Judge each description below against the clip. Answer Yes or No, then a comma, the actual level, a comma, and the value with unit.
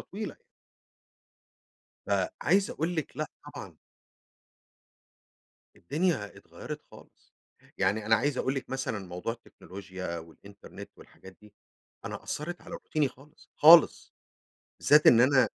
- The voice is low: Yes, low, 130 Hz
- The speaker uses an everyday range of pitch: No, wide, 7.2 semitones